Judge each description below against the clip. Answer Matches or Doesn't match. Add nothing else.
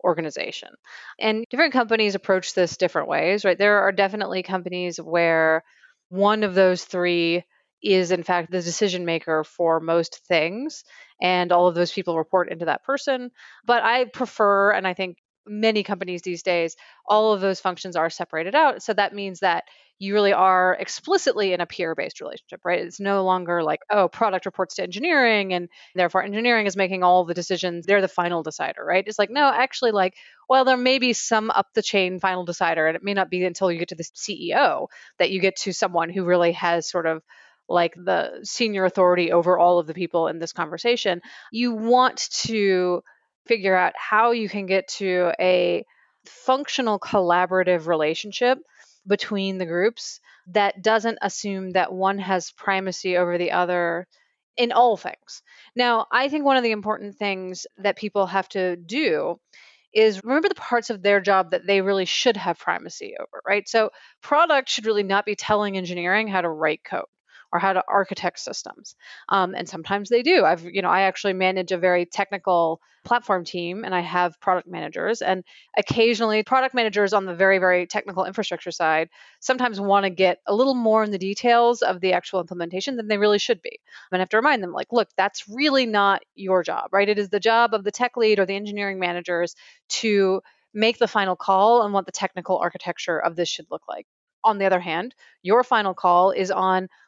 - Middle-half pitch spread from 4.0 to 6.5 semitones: Doesn't match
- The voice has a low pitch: Doesn't match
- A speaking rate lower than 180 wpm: Doesn't match